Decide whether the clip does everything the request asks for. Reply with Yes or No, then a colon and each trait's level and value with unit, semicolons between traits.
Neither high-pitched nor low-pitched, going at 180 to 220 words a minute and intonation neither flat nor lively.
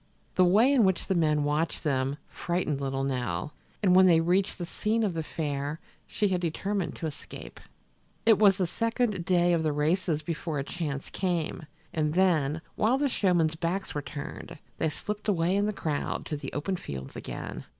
Yes: medium, 170 Hz; average, 190 wpm; average, 4.2 semitones